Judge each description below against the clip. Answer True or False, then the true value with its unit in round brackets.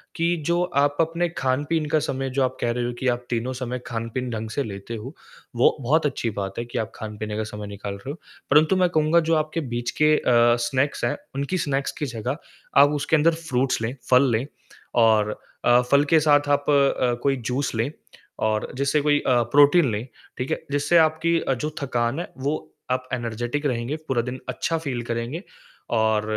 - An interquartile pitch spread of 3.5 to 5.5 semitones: True (4.1 semitones)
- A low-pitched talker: True (130 Hz)